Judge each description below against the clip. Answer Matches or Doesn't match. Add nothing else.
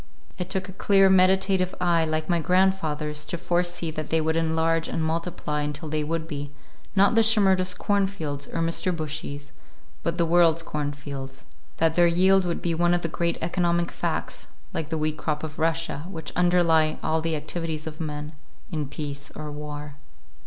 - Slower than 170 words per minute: Doesn't match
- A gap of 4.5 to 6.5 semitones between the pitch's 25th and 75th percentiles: Doesn't match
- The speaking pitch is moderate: Matches